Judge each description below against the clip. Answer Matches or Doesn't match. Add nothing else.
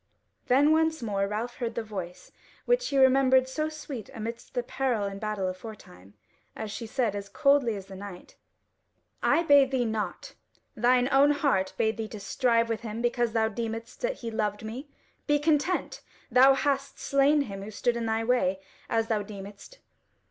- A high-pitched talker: Matches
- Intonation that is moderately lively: Matches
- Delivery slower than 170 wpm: Doesn't match